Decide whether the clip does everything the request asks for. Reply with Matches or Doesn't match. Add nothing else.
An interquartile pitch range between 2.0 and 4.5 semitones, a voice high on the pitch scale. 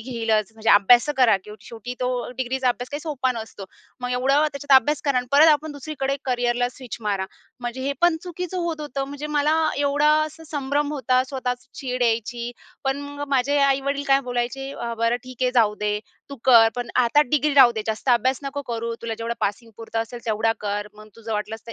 Matches